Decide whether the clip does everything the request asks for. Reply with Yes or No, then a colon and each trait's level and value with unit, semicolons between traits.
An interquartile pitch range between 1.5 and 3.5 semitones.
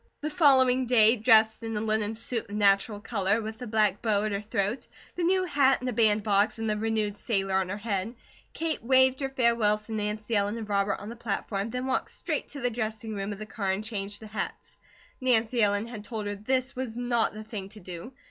Yes: average, 2.8 semitones